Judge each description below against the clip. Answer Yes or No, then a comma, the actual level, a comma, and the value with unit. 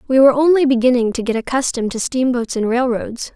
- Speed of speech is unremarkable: Yes, average, 195 wpm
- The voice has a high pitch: Yes, very high, 250 Hz